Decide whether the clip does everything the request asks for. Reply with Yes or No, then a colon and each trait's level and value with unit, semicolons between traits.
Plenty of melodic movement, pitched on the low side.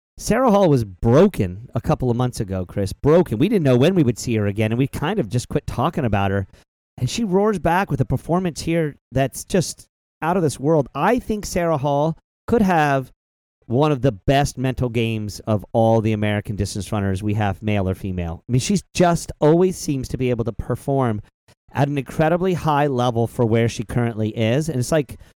Yes: wide, 5.9 semitones; low, 125 Hz